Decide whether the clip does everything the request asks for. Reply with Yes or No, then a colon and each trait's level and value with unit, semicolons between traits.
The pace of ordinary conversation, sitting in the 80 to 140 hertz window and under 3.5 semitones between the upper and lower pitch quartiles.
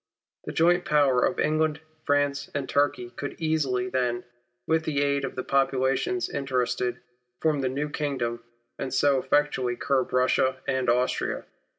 Yes: average, 150 wpm; low, 135 Hz; narrow, 2.5 semitones